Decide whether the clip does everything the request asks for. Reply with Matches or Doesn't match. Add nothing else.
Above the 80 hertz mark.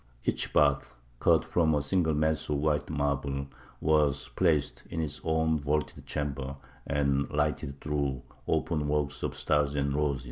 Doesn't match